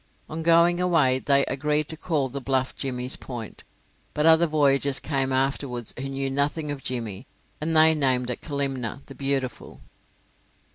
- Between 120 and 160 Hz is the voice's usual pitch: Yes, medium, 140 Hz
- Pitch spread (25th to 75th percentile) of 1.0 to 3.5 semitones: Yes, average, 2.7 semitones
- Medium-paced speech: Yes, average, 155 wpm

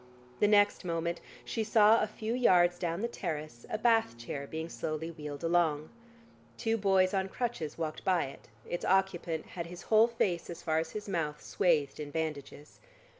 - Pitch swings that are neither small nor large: Yes, average, 4.6 semitones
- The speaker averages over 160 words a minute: Yes, average, 175 wpm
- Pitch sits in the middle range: Yes, medium, 175 Hz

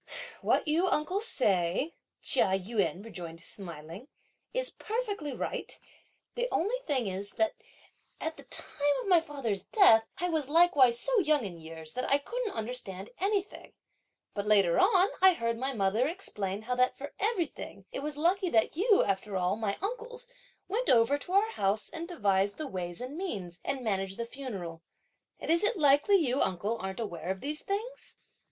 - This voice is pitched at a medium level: No, very high, 260 Hz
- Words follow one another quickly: No, average, 175 wpm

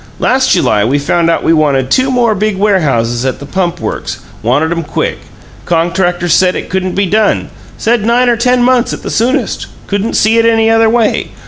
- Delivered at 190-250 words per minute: Yes, average, 200 wpm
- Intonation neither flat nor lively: No, wide, 5.8 semitones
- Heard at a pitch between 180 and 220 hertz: Yes, high, 190 Hz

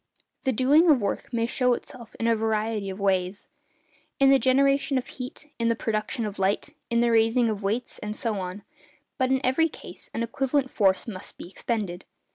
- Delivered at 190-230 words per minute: Yes, average, 195 wpm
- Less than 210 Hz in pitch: No, high, 230 Hz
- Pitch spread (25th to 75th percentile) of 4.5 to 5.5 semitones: No, average, 3.7 semitones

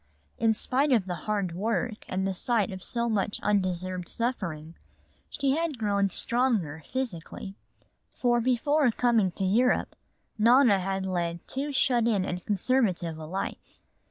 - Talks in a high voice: Yes, high, 210 Hz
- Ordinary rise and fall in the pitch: Yes, average, 4.8 semitones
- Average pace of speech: Yes, average, 145 wpm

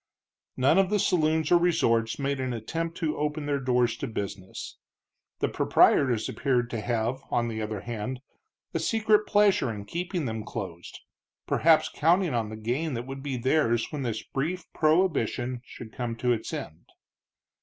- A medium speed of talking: Yes, average, 165 wpm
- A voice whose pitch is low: Yes, low, 130 Hz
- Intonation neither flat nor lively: No, wide, 5.7 semitones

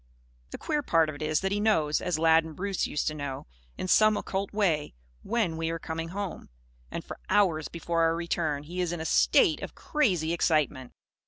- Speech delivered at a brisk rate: Yes, fast, 210 wpm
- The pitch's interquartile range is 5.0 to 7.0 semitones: No, average, 3.8 semitones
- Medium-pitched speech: Yes, medium, 165 Hz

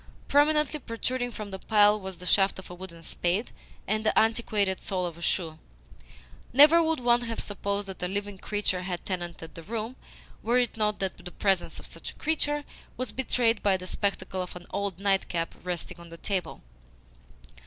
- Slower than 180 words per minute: No, average, 185 wpm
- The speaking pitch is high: Yes, high, 200 Hz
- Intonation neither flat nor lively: Yes, average, 4.0 semitones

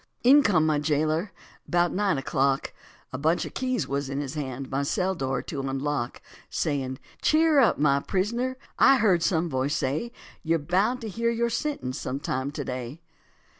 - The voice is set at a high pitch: No, medium, 155 Hz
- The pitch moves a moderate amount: No, wide, 7.3 semitones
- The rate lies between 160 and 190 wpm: Yes, average, 175 wpm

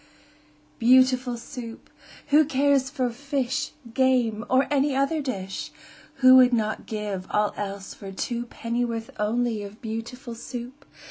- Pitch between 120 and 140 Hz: No, high, 245 Hz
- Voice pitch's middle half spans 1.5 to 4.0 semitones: Yes, average, 2.9 semitones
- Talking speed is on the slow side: Yes, slow, 130 wpm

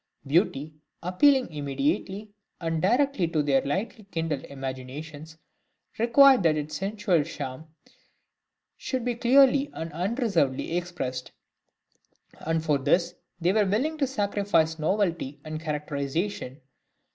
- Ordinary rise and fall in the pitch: No, wide, 5.9 semitones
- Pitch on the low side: No, medium, 165 Hz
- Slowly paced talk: Yes, slow, 110 wpm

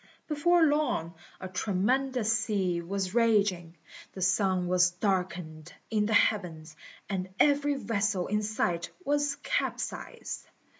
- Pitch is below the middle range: No, high, 200 Hz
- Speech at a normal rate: No, slow, 115 wpm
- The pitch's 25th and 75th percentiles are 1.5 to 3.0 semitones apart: No, average, 4.6 semitones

